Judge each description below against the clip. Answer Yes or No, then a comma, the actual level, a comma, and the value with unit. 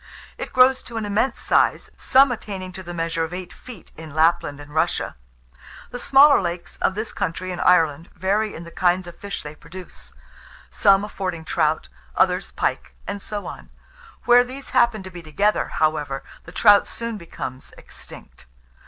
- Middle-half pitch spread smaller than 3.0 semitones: No, average, 4.4 semitones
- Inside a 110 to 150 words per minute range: No, average, 170 wpm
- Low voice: No, medium, 185 Hz